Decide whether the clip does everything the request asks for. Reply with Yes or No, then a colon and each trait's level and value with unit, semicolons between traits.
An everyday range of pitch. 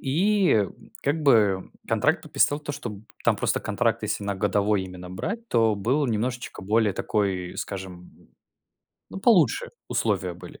No: wide, 6.7 semitones